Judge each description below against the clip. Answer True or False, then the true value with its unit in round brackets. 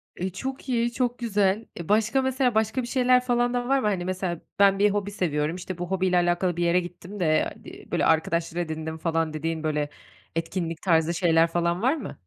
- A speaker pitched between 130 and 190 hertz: True (185 Hz)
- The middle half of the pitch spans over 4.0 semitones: True (5.5 semitones)